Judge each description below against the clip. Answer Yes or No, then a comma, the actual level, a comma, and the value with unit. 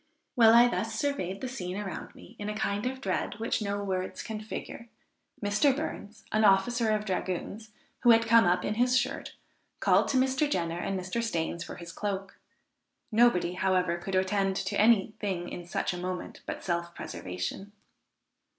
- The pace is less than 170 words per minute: No, average, 180 wpm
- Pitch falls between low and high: No, high, 205 Hz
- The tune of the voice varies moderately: Yes, average, 3.7 semitones